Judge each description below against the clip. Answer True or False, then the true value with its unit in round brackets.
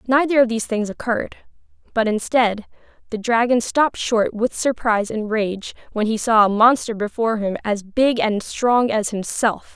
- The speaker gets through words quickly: False (170 wpm)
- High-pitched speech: True (225 Hz)